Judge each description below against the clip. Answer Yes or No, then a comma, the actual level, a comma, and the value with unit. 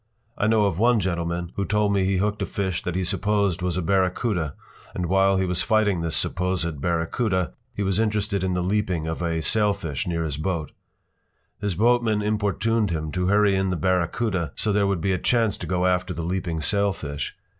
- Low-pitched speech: Yes, very low, 95 Hz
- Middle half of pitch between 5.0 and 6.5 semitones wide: No, average, 3.3 semitones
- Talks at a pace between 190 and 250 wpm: Yes, average, 200 wpm